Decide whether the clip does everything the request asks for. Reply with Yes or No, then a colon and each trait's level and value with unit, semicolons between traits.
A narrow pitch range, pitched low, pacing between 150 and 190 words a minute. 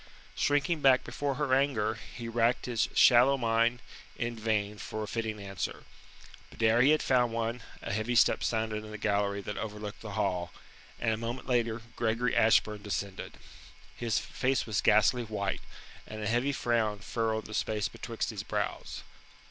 Yes: narrow, 2.3 semitones; low, 115 Hz; average, 170 wpm